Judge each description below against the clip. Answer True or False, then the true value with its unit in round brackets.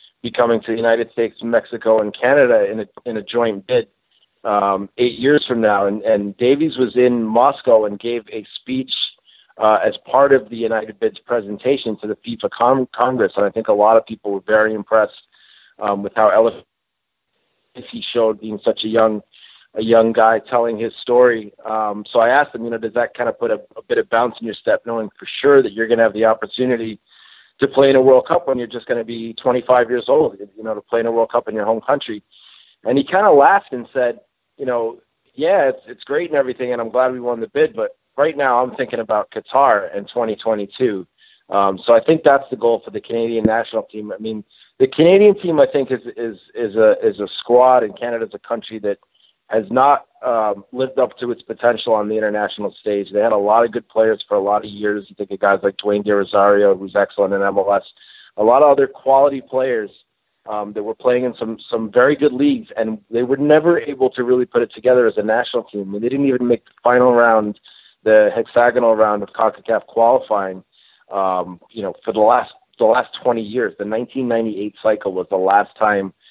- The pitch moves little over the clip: False (3.0 semitones)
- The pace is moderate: False (225 wpm)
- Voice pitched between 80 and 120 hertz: True (115 Hz)